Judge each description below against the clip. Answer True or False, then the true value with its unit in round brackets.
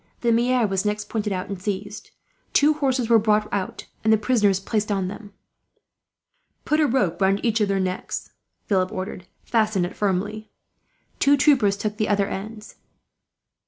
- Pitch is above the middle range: True (210 Hz)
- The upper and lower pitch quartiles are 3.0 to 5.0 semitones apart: False (2.6 semitones)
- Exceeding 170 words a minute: False (165 wpm)